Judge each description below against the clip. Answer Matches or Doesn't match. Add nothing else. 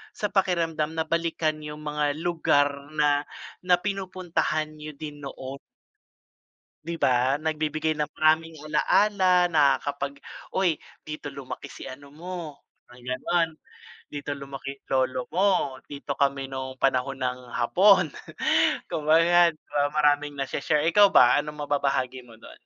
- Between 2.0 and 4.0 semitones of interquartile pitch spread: Matches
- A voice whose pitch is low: Doesn't match